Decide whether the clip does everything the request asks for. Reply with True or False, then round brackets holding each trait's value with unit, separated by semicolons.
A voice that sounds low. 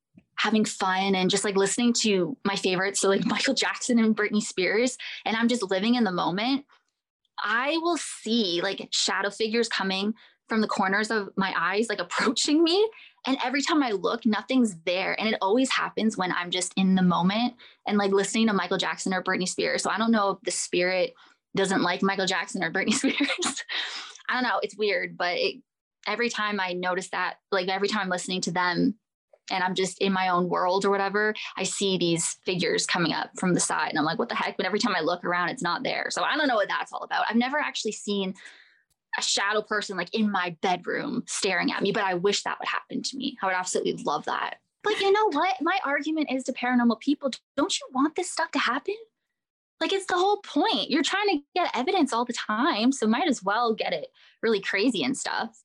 False (220 Hz)